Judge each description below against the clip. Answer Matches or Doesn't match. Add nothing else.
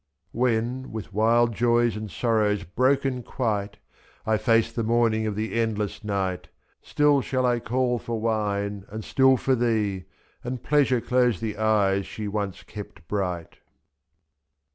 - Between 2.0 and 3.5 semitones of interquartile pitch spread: Matches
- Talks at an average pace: Matches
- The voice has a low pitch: Matches